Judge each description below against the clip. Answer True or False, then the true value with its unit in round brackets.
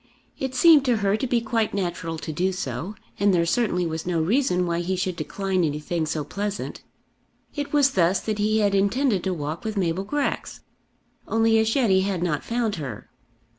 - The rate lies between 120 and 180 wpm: False (195 wpm)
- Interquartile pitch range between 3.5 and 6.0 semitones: True (4.7 semitones)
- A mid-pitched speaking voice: False (195 Hz)